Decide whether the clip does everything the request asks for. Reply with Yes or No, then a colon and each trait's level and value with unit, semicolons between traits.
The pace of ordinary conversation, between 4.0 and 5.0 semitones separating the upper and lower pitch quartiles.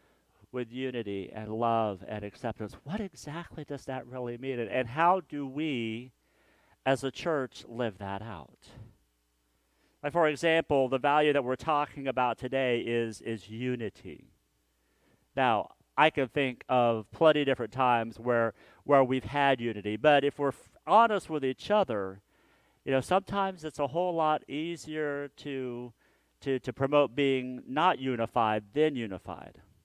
Yes: average, 150 wpm; average, 4.3 semitones